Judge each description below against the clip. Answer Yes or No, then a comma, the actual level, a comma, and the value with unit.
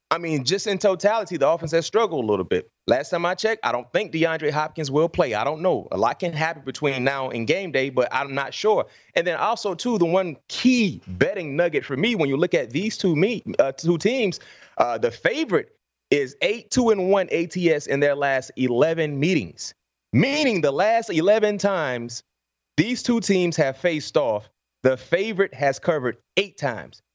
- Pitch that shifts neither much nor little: No, wide, 7.5 semitones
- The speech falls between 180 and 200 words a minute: Yes, average, 195 wpm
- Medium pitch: Yes, medium, 170 Hz